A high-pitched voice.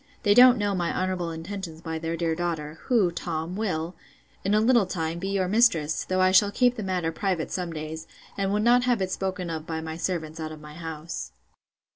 No: medium, 180 Hz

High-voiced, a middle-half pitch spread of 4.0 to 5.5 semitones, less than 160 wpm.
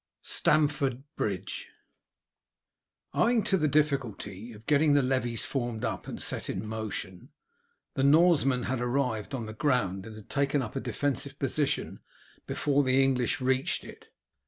No: low, 130 Hz; average, 4.3 semitones; average, 145 wpm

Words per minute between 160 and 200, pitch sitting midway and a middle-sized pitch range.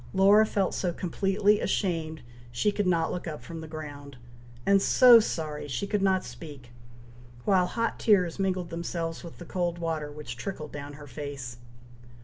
Yes: average, 165 wpm; medium, 170 Hz; average, 4.5 semitones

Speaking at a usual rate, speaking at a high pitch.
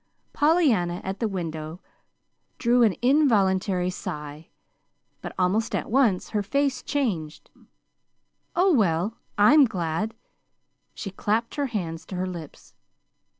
No: slow, 120 wpm; high, 205 Hz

